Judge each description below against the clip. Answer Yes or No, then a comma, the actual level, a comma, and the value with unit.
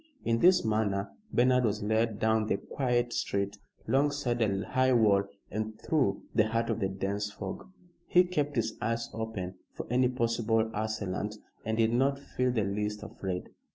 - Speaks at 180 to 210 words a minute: No, average, 165 wpm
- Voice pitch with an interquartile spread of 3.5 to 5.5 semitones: No, average, 2.9 semitones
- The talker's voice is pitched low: Yes, low, 110 Hz